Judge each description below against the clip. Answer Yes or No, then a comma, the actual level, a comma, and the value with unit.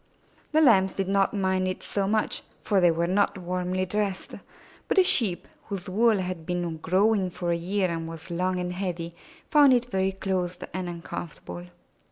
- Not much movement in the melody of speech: Yes, narrow, 2.3 semitones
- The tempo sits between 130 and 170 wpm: No, average, 180 wpm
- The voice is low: No, medium, 185 Hz